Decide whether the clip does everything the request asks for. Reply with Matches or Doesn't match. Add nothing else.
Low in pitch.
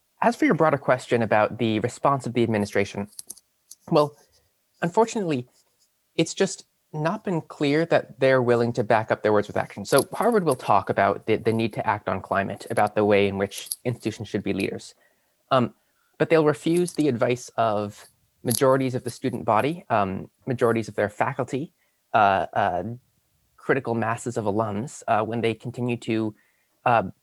Matches